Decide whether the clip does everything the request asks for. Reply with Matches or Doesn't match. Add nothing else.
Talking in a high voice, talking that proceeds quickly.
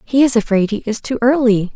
Matches